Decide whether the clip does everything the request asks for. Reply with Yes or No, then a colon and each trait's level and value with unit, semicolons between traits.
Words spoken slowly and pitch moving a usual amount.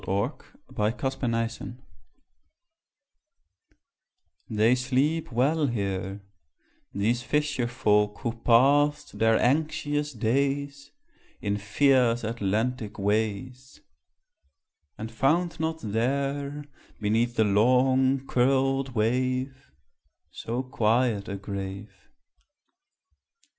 Yes: slow, 85 wpm; average, 4.1 semitones